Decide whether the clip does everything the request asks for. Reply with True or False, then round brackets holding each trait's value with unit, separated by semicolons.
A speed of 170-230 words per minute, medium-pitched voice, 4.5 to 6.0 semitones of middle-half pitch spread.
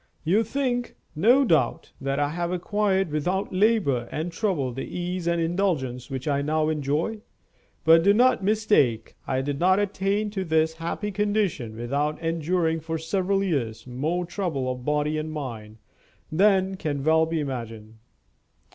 False (155 wpm; 165 Hz; 5.3 semitones)